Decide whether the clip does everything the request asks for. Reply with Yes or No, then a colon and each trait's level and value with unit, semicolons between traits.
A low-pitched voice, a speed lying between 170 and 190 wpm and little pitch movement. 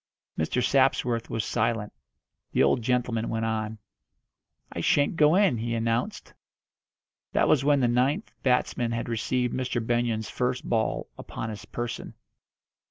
No: low, 120 Hz; average, 140 wpm; narrow, 2.2 semitones